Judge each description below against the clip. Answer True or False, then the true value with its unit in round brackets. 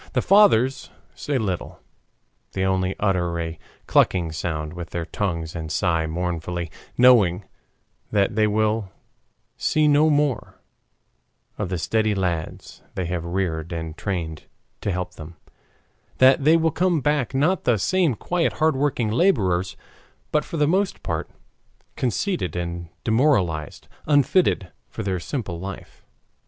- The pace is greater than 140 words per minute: False (135 wpm)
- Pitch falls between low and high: False (95 Hz)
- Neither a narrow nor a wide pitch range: False (8.3 semitones)